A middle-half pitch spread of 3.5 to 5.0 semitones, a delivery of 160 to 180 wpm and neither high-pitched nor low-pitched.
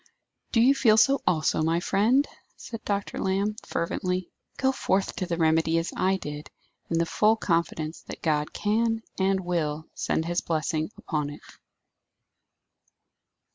No: average, 4.6 semitones; average, 145 wpm; medium, 180 Hz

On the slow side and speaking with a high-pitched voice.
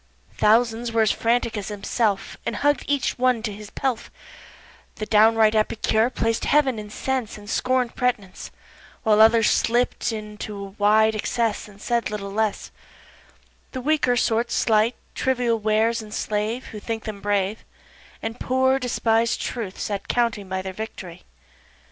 No: average, 145 wpm; high, 225 Hz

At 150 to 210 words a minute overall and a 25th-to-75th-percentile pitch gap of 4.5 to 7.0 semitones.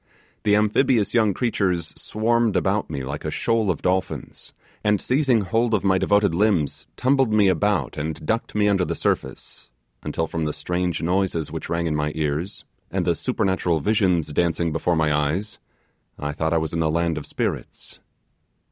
Yes: average, 180 wpm; average, 4.8 semitones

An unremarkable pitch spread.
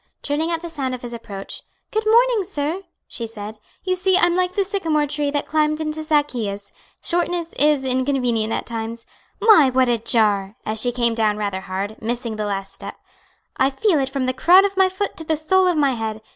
No: wide, 7.1 semitones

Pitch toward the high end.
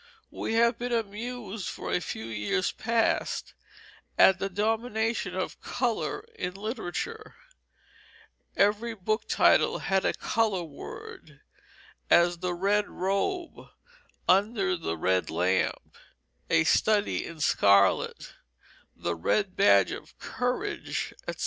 Yes: high, 200 Hz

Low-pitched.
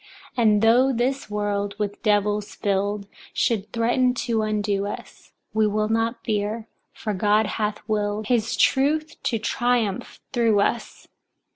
No: high, 215 Hz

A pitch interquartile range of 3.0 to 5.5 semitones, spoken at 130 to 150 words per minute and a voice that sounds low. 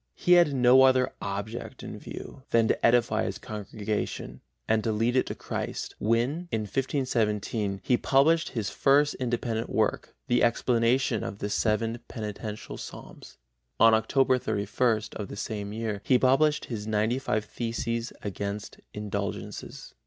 Yes: average, 3.3 semitones; average, 145 wpm; low, 115 Hz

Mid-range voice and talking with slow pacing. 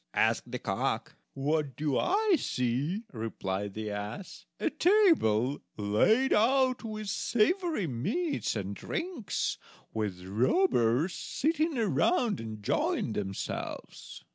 Yes: medium, 160 Hz; slow, 105 wpm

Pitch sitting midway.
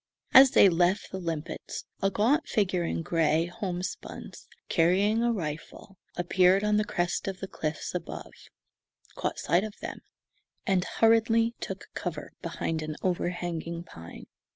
Yes: medium, 180 Hz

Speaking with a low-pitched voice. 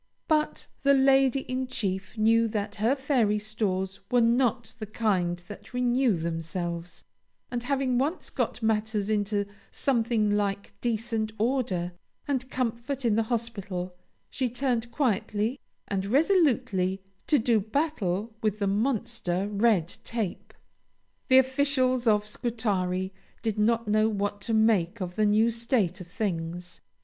No: high, 220 Hz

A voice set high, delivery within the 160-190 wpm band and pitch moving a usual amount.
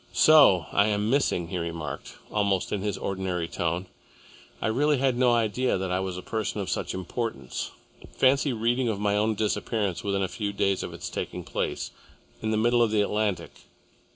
No: low, 105 Hz; average, 185 wpm; average, 3.6 semitones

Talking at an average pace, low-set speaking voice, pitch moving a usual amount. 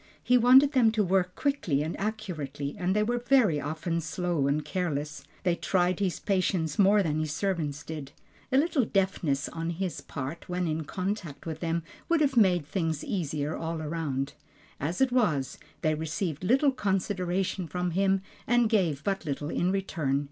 No: average, 170 wpm; medium, 180 Hz; average, 4.5 semitones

